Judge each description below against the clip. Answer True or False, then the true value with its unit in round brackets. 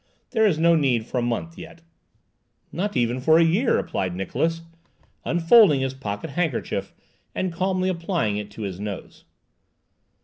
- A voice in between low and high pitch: True (160 Hz)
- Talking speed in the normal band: True (150 wpm)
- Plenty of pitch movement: True (6.9 semitones)